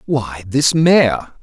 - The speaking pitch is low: Yes, low, 130 Hz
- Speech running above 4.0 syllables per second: No, 2.5 syllables/s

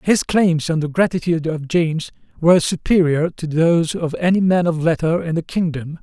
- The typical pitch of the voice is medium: Yes, medium, 165 Hz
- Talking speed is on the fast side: No, average, 190 wpm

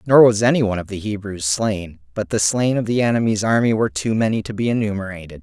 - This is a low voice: Yes, low, 105 Hz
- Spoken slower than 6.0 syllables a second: No, 6.3 syllables/s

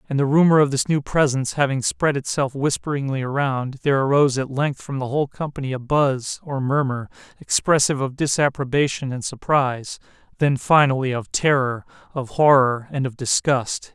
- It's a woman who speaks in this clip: No, male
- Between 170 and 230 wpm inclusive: No, average, 160 wpm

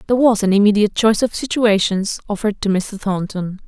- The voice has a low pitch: No, high, 205 Hz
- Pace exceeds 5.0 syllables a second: Yes, 6.2 syllables/s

